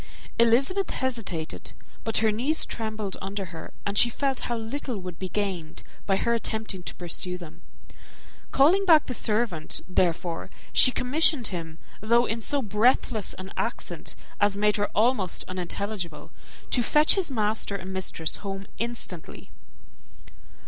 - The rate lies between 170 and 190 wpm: No, average, 140 wpm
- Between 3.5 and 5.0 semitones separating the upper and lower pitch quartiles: Yes, average, 4.4 semitones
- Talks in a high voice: Yes, high, 210 Hz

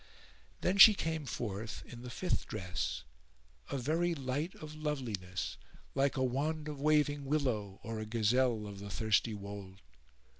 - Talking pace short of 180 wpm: Yes, average, 150 wpm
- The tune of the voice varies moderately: No, wide, 6.1 semitones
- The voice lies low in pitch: Yes, low, 130 Hz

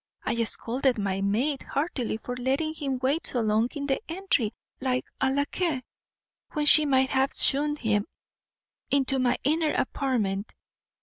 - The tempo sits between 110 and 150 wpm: Yes, average, 145 wpm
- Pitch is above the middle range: Yes, very high, 265 Hz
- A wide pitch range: No, average, 3.7 semitones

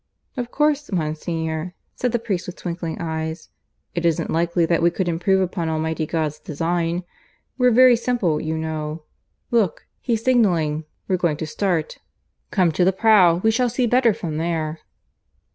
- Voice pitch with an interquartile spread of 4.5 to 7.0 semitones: Yes, average, 5.2 semitones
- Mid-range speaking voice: Yes, medium, 170 Hz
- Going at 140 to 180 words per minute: Yes, average, 160 wpm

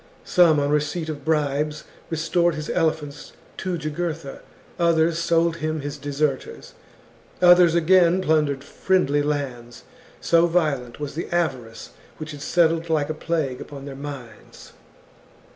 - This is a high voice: No, medium, 155 Hz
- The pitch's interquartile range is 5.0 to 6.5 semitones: No, average, 2.7 semitones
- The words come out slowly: Yes, slow, 130 wpm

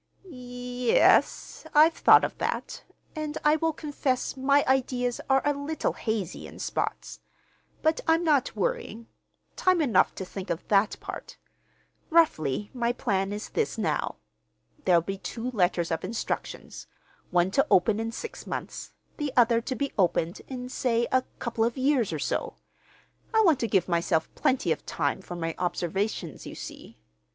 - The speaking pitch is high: Yes, high, 240 Hz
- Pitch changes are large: Yes, wide, 6.9 semitones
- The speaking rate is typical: Yes, average, 160 wpm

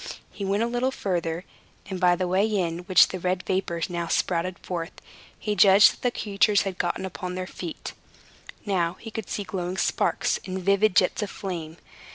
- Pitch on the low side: No, medium, 185 Hz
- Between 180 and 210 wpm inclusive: Yes, average, 190 wpm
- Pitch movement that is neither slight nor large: No, narrow, 2.1 semitones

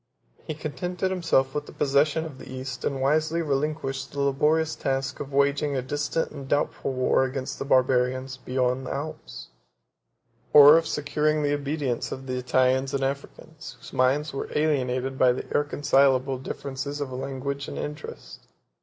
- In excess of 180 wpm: No, average, 160 wpm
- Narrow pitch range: Yes, narrow, 2.1 semitones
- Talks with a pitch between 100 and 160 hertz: Yes, medium, 140 Hz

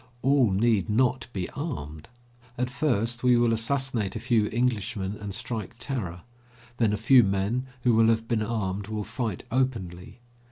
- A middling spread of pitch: Yes, average, 3.5 semitones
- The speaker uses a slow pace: No, average, 160 wpm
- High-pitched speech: No, low, 115 Hz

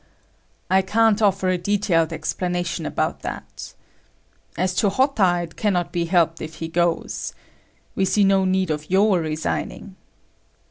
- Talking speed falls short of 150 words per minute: Yes, slow, 135 wpm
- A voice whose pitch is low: No, medium, 185 Hz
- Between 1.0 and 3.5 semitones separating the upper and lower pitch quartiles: Yes, average, 2.9 semitones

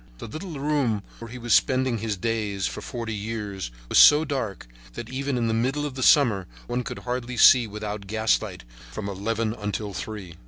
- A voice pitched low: Yes, low, 115 Hz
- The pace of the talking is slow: No, average, 190 wpm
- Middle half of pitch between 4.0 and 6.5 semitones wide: No, average, 3.6 semitones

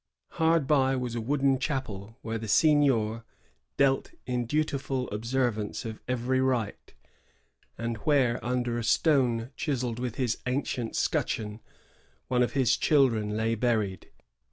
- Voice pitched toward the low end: Yes, low, 125 Hz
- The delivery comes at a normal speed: No, slow, 130 wpm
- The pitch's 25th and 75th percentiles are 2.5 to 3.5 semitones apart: Yes, average, 2.9 semitones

